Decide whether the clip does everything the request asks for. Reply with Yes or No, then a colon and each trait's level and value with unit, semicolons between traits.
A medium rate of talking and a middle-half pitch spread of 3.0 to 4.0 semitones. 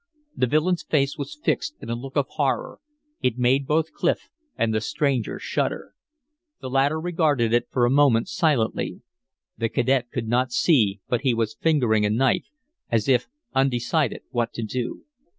Yes: average, 170 wpm; average, 3.7 semitones